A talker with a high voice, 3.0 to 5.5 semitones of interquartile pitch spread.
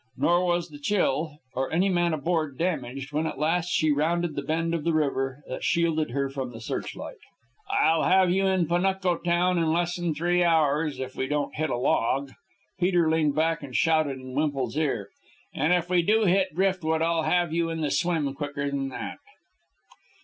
No: medium, 160 Hz; average, 3.6 semitones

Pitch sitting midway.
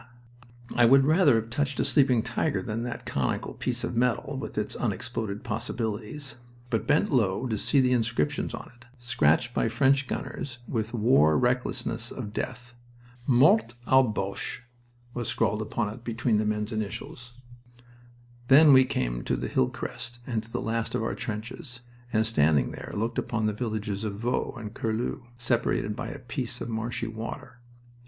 No: low, 115 Hz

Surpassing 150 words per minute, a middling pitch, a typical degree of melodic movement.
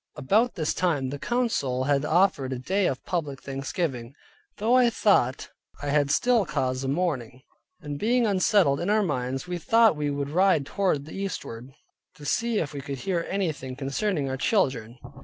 No: average, 175 wpm; medium, 150 Hz; wide, 6.6 semitones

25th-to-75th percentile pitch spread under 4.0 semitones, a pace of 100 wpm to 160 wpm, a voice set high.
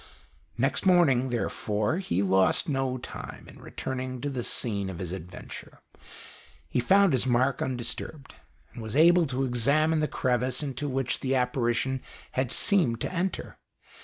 No: average, 3.5 semitones; average, 150 wpm; low, 130 Hz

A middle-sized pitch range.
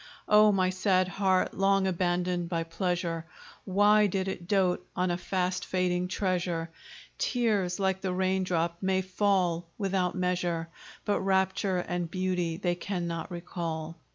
No: narrow, 1.5 semitones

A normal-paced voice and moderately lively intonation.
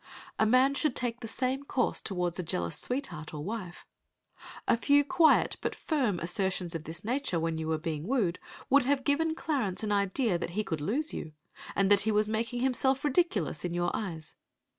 No: average, 195 wpm; wide, 7.3 semitones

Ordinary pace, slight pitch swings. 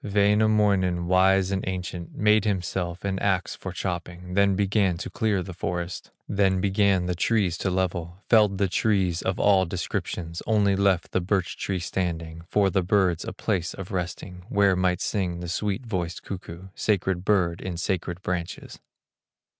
Yes: average, 160 wpm; narrow, 2.1 semitones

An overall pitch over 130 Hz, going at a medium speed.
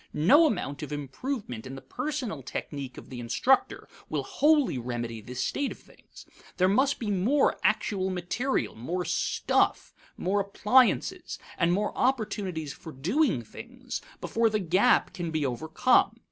Yes: medium, 185 Hz; average, 145 wpm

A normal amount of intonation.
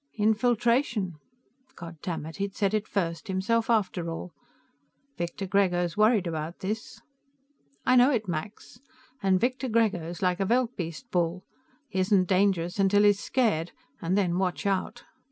Yes: average, 3.8 semitones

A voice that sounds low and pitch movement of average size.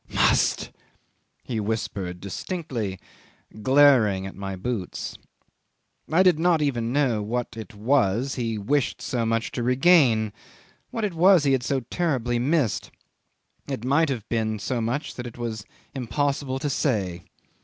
Yes: low, 120 Hz; average, 4.6 semitones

